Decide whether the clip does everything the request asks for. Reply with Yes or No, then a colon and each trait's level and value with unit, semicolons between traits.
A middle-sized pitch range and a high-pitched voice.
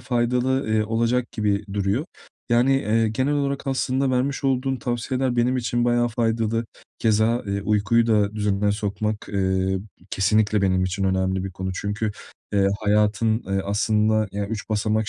No: average, 3.0 semitones; low, 110 Hz